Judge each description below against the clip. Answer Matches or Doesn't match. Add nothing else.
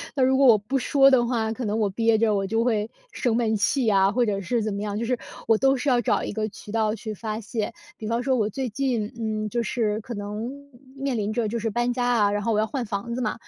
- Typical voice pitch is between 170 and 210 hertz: Doesn't match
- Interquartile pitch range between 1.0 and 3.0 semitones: Matches